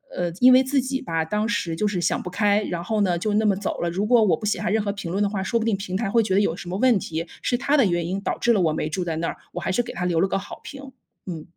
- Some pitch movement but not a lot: Yes, average, 4.0 semitones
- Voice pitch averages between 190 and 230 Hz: Yes, high, 200 Hz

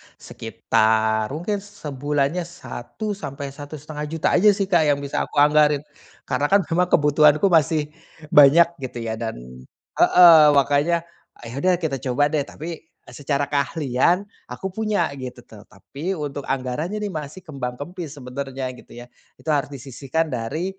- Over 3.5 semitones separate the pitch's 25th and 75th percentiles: Yes, average, 3.9 semitones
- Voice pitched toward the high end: No, medium, 150 Hz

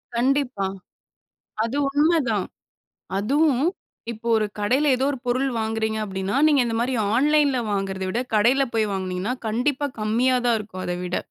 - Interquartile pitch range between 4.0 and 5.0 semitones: Yes, average, 4.4 semitones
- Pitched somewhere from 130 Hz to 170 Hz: No, high, 235 Hz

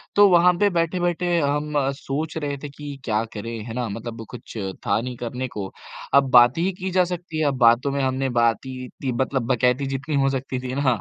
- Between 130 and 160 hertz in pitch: Yes, low, 135 Hz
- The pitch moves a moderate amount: Yes, average, 3.9 semitones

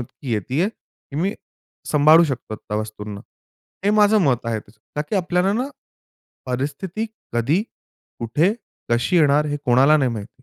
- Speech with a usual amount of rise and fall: No, wide, 7.1 semitones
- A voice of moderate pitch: Yes, medium, 145 Hz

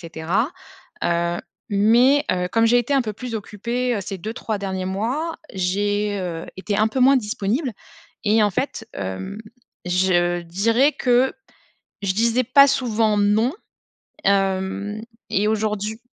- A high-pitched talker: Yes, high, 210 Hz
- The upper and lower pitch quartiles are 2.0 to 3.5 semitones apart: No, average, 3.9 semitones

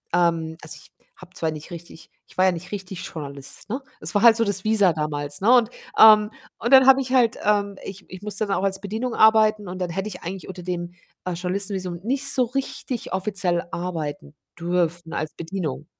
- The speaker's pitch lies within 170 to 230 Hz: Yes, high, 190 Hz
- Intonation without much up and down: No, average, 3.9 semitones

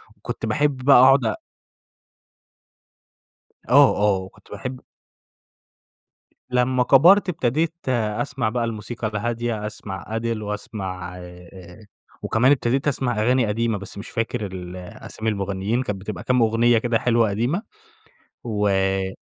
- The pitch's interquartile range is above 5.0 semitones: No, average, 3.7 semitones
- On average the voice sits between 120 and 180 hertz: No, low, 110 Hz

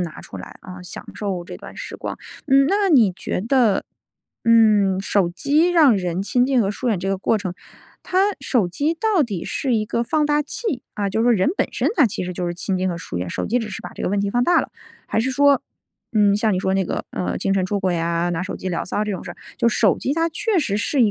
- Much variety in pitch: Yes, wide, 6.1 semitones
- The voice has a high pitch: Yes, high, 210 Hz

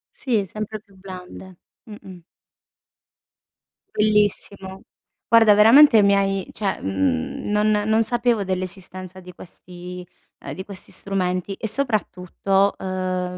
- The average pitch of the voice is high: Yes, high, 195 Hz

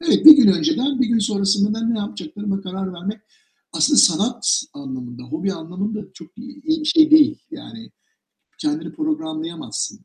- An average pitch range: No, wide, 7.9 semitones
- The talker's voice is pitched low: No, high, 225 Hz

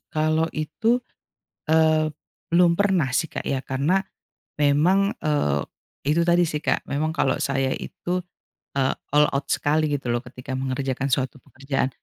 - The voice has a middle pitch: Yes, medium, 150 Hz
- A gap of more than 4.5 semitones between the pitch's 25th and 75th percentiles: No, average, 3.2 semitones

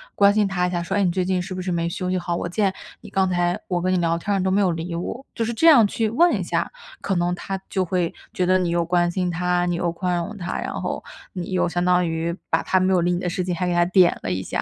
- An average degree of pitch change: No, narrow, 1.5 semitones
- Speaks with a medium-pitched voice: Yes, medium, 180 Hz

